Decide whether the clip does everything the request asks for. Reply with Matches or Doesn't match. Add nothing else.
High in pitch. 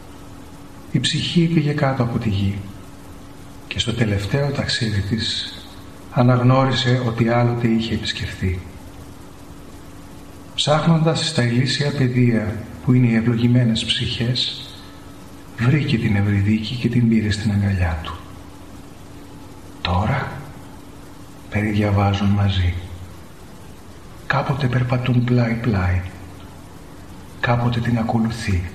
Doesn't match